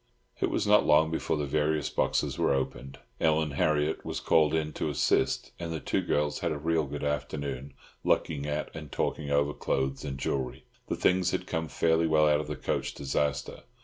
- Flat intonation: Yes, narrow, 1.8 semitones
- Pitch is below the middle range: Yes, very low, 75 Hz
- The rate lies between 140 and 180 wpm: No, average, 195 wpm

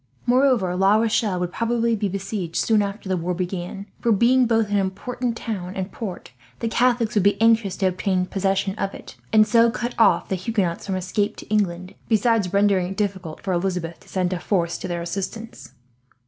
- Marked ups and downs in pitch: No, average, 3.5 semitones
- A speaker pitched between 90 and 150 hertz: No, high, 200 Hz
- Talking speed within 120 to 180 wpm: No, average, 195 wpm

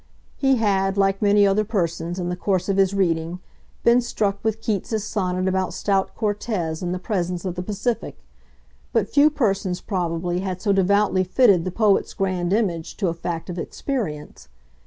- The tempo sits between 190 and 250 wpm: No, average, 175 wpm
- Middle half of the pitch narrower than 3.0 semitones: Yes, narrow, 2.6 semitones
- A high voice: Yes, high, 195 Hz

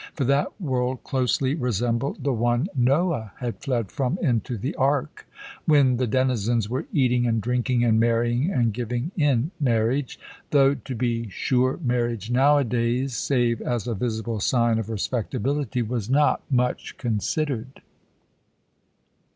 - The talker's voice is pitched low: Yes, low, 125 Hz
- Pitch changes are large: No, narrow, 2.6 semitones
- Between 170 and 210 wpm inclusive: No, slow, 135 wpm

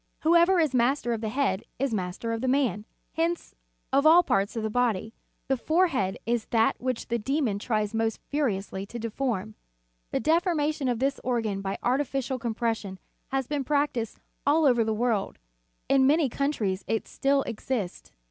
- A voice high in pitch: Yes, high, 245 Hz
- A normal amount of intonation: Yes, average, 4.3 semitones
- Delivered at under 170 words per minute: No, average, 175 wpm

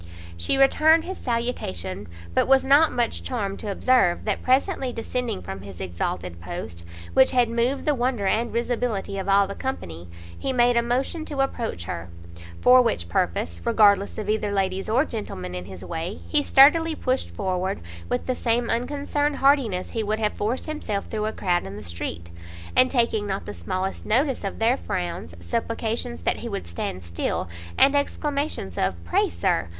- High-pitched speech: Yes, high, 220 Hz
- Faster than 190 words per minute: No, average, 175 wpm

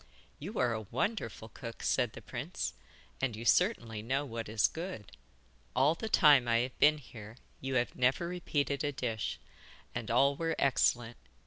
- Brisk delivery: No, average, 165 wpm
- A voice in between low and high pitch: No, low, 130 Hz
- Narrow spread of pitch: No, average, 4.4 semitones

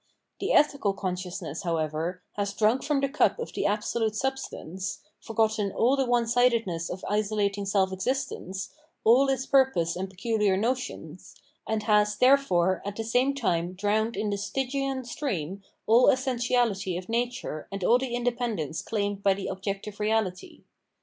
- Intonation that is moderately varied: Yes, average, 4.5 semitones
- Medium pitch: No, high, 210 Hz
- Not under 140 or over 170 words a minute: Yes, average, 150 wpm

